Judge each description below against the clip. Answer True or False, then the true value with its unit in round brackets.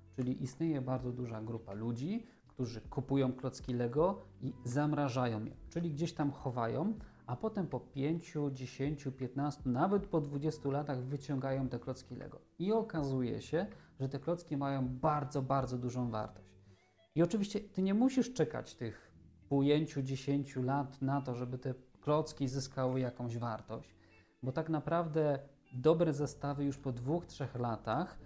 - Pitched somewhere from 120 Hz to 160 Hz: True (135 Hz)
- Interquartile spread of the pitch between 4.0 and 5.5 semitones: False (3.2 semitones)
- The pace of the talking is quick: False (145 wpm)